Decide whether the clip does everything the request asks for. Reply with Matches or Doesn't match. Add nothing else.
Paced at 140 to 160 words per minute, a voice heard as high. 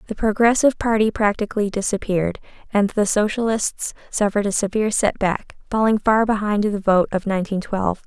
Matches